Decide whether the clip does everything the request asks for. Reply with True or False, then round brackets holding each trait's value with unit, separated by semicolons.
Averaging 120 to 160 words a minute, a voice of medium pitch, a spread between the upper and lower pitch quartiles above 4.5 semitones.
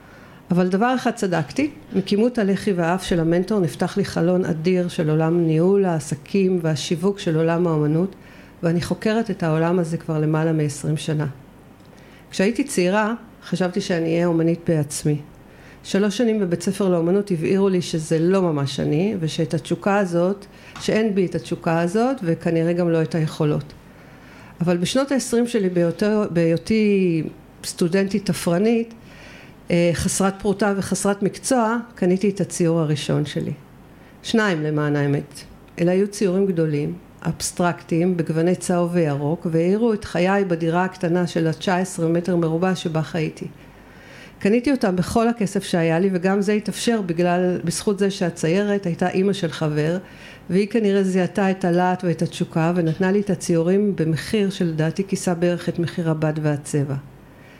False (140 wpm; 180 Hz; 3.1 semitones)